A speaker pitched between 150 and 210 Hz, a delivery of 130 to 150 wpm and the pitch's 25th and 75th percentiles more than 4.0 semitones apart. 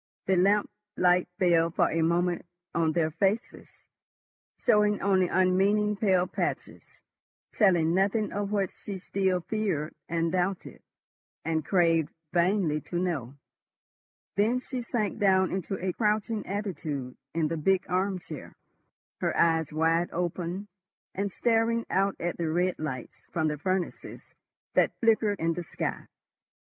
No: medium, 185 Hz; slow, 135 wpm; average, 3.4 semitones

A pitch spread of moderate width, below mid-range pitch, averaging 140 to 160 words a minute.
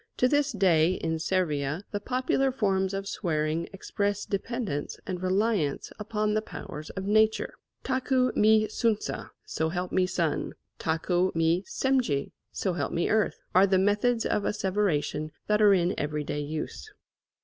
No: average, 4.8 semitones; high, 190 Hz; average, 150 wpm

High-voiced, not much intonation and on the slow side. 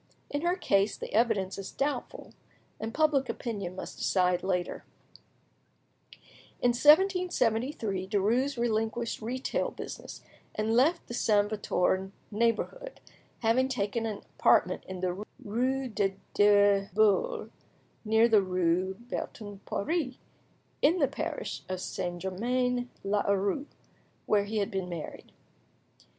No: high, 220 Hz; average, 4.5 semitones; slow, 120 wpm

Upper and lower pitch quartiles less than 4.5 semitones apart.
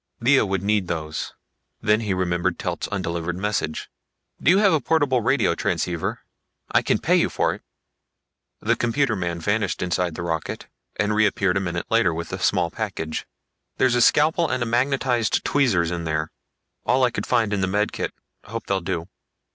No: wide, 5.4 semitones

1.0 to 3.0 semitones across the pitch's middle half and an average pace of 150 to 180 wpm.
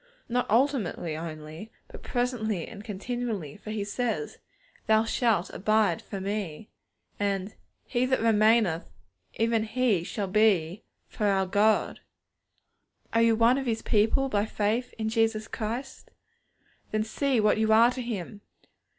No: narrow, 2.6 semitones; average, 140 wpm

